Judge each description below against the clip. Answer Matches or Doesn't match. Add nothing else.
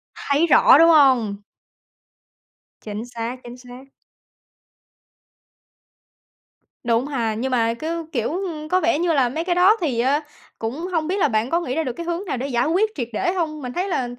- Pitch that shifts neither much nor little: Doesn't match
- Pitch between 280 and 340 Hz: Matches